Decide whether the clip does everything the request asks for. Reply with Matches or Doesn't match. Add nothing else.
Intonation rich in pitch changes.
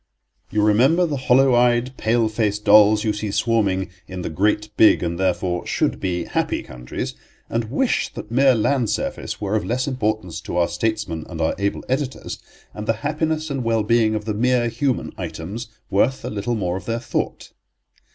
Doesn't match